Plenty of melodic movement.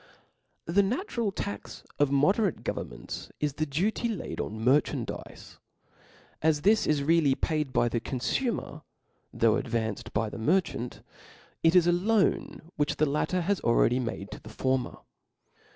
Yes: wide, 7.2 semitones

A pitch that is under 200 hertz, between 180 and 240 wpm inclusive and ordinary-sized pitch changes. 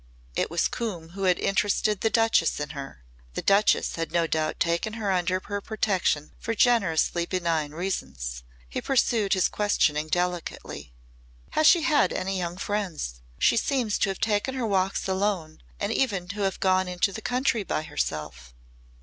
No: medium, 185 Hz; average, 165 wpm; average, 4.3 semitones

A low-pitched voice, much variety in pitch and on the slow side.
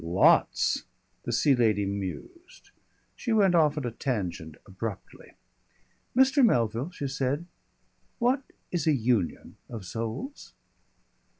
Yes: low, 125 Hz; wide, 9.0 semitones; slow, 115 wpm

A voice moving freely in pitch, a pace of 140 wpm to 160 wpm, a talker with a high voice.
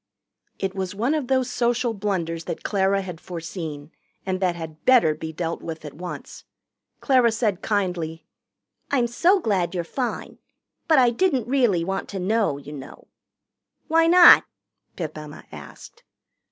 Yes: wide, 6.5 semitones; average, 155 wpm; high, 195 Hz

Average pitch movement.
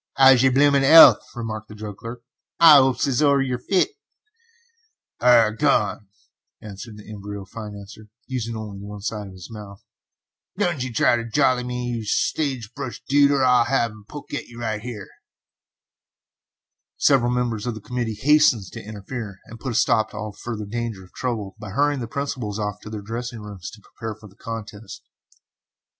Yes: average, 3.5 semitones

